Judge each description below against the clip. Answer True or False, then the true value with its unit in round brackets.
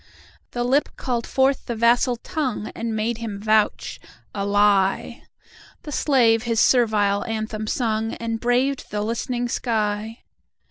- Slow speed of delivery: True (110 wpm)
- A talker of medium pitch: False (230 Hz)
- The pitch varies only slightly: True (2.3 semitones)